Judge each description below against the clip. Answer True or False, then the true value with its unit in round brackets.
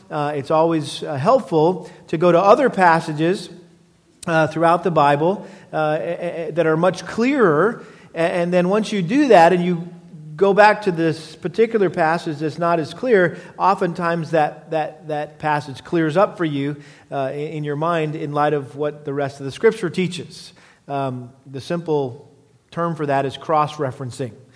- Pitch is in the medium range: True (160 Hz)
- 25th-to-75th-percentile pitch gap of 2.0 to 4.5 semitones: True (2.9 semitones)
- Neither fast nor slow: True (180 wpm)